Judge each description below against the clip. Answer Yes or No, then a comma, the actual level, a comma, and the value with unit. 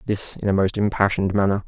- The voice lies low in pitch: Yes, low, 100 Hz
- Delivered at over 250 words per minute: No, fast, 215 wpm